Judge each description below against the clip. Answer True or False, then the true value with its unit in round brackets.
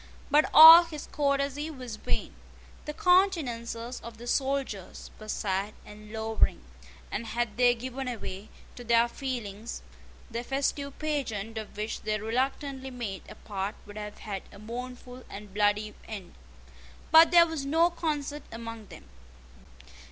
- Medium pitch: False (240 Hz)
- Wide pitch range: False (4.8 semitones)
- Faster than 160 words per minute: False (145 wpm)